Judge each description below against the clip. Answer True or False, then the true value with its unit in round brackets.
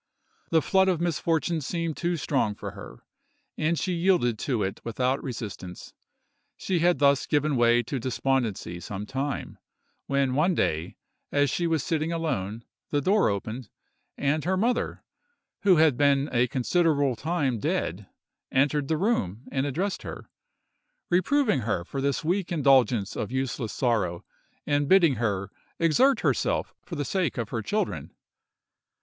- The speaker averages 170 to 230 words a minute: False (150 wpm)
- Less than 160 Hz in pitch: True (140 Hz)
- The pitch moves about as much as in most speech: False (5.9 semitones)